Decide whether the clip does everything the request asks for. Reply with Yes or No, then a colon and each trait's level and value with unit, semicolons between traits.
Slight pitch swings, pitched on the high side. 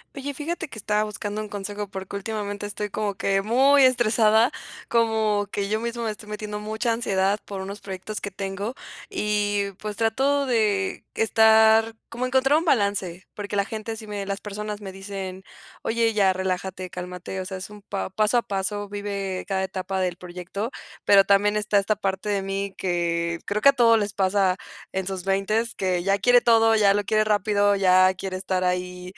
Yes: narrow, 2.3 semitones; high, 205 Hz